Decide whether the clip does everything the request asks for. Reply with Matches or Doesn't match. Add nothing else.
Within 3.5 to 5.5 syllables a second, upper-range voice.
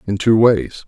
Doesn't match